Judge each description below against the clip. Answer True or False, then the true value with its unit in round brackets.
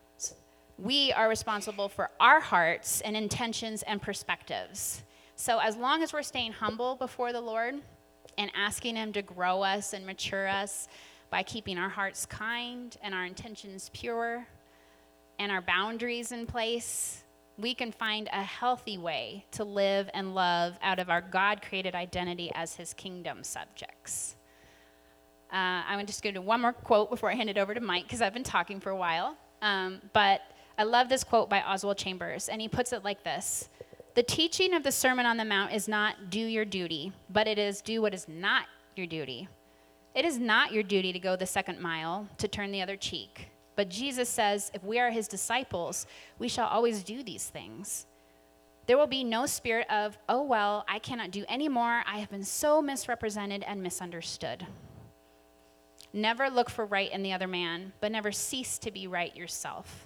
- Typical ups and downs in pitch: True (4.0 semitones)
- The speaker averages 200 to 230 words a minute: False (185 wpm)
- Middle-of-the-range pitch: False (205 Hz)